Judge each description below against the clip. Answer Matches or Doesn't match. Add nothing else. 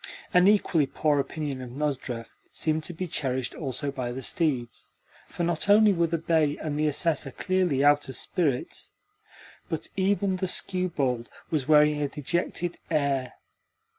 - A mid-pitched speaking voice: Matches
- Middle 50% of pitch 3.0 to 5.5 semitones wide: Matches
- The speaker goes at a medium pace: Matches